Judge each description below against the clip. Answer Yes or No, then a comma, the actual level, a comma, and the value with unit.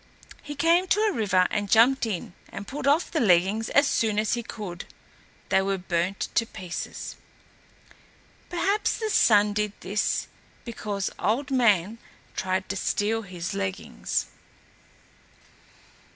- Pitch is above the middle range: Yes, high, 210 Hz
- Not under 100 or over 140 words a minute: Yes, slow, 135 wpm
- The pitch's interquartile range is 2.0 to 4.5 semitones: No, average, 5.2 semitones